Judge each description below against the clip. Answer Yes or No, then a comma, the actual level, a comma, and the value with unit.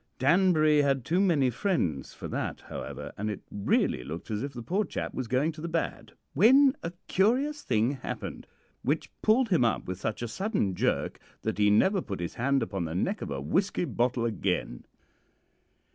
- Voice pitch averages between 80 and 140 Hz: Yes, low, 135 Hz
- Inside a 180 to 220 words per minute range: Yes, average, 190 wpm